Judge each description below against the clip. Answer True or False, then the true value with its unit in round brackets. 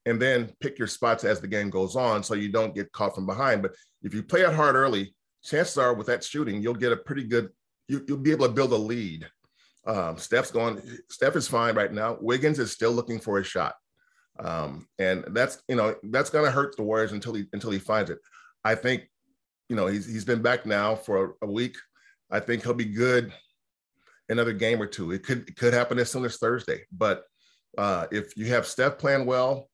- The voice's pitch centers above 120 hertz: False (115 Hz)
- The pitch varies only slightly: False (3.4 semitones)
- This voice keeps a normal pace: False (225 wpm)